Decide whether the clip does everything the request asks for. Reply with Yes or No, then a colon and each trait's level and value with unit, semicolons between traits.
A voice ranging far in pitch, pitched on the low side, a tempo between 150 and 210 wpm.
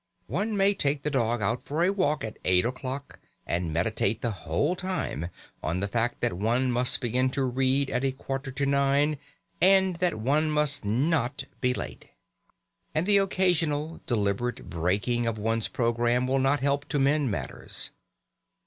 No: average, 4.3 semitones; low, 130 Hz; average, 165 wpm